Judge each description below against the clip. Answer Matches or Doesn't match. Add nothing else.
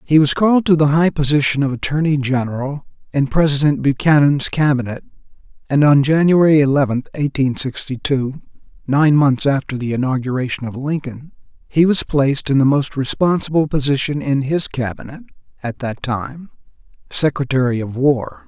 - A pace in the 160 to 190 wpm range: Doesn't match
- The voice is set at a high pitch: Doesn't match